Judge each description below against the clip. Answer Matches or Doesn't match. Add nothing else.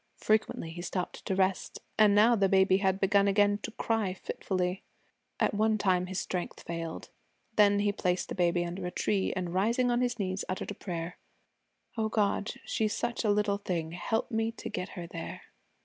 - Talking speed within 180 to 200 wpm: Matches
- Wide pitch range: Doesn't match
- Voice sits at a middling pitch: Doesn't match